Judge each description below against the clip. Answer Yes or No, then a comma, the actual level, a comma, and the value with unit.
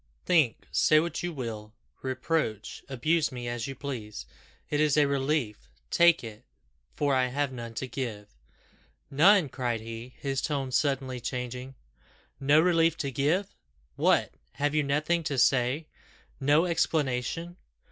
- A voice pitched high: No, low, 135 Hz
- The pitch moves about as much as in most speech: Yes, average, 3.7 semitones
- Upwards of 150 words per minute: No, average, 140 wpm